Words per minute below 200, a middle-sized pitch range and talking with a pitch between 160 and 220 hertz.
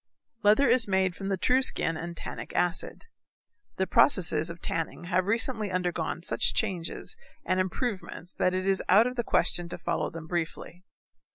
Yes: average, 170 wpm; average, 3.5 semitones; medium, 185 Hz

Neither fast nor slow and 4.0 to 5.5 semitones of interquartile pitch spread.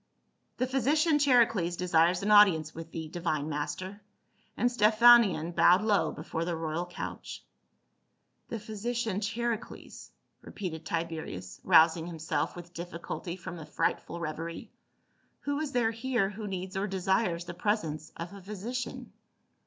Yes: average, 150 wpm; average, 4.9 semitones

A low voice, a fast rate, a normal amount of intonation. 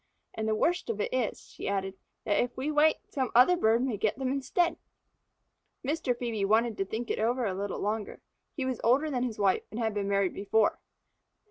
No: high, 230 Hz; fast, 210 wpm; average, 4.0 semitones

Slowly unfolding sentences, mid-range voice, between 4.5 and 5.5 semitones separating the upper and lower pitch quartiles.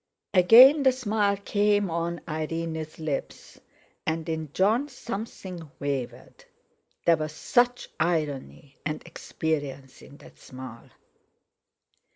Yes: slow, 105 wpm; medium, 165 Hz; average, 5.1 semitones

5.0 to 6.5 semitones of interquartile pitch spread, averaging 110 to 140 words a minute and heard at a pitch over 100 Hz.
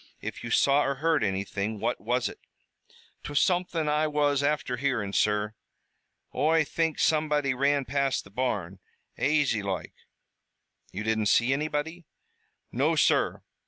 Yes: wide, 5.5 semitones; slow, 135 wpm; medium, 140 Hz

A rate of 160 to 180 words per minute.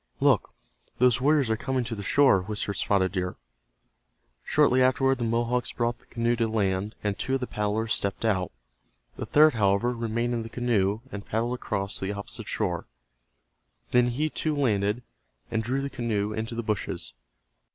Yes: average, 175 wpm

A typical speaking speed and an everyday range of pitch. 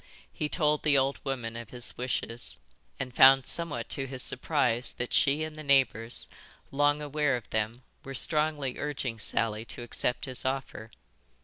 Yes: average, 165 wpm; average, 3.4 semitones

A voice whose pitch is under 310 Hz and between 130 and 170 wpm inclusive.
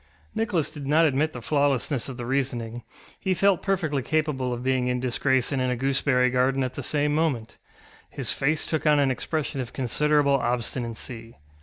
No: low, 135 Hz; average, 180 wpm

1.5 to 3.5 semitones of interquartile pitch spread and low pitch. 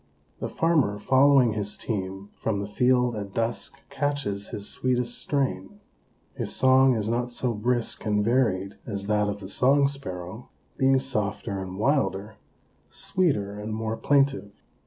No: average, 4.4 semitones; low, 110 Hz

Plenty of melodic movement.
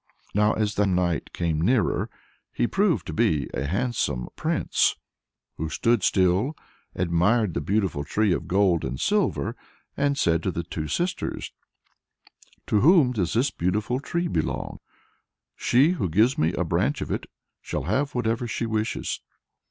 Yes: wide, 6.5 semitones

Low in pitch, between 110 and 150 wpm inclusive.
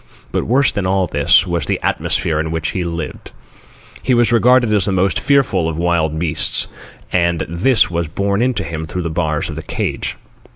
No: very low, 90 Hz; average, 200 wpm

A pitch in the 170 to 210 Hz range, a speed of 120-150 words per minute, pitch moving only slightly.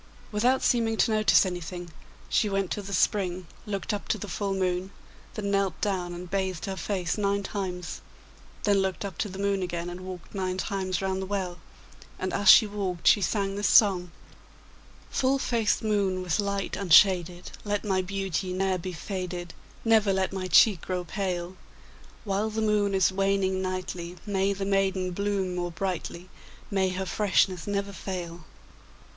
No: high, 190 Hz; average, 170 wpm; narrow, 1.7 semitones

